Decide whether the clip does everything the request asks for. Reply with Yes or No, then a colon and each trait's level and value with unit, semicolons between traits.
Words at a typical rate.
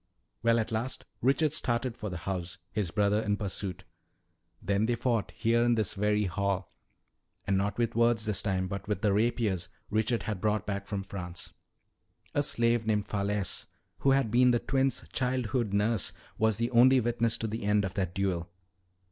Yes: average, 180 wpm